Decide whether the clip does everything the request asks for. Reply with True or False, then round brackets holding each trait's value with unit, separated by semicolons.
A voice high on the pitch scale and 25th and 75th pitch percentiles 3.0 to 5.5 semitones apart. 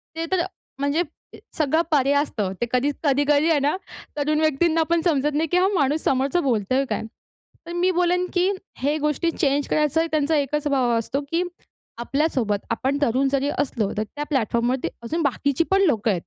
True (290 Hz; 3.5 semitones)